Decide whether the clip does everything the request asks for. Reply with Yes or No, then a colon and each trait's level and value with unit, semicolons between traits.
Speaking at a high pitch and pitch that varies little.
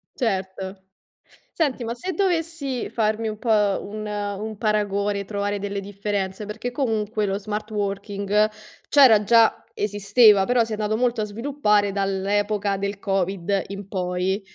Yes: high, 205 Hz; narrow, 2.0 semitones